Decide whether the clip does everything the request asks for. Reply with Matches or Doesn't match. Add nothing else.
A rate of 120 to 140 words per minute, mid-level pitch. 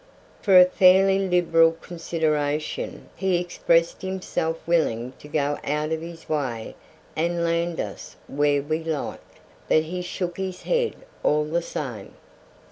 Matches